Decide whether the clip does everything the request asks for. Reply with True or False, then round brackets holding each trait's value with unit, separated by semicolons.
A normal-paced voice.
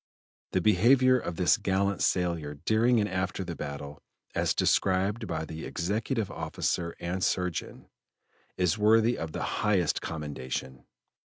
False (130 wpm)